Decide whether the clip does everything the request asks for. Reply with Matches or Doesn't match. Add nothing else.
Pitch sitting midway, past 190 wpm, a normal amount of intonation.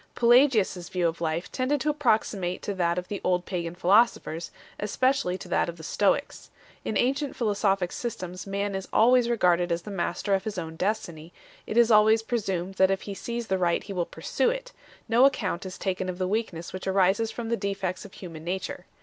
Doesn't match